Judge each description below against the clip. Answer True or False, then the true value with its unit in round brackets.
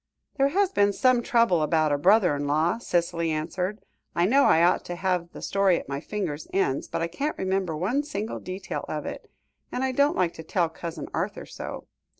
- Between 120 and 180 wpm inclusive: False (205 wpm)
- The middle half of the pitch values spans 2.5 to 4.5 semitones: False (5.3 semitones)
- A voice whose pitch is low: False (185 Hz)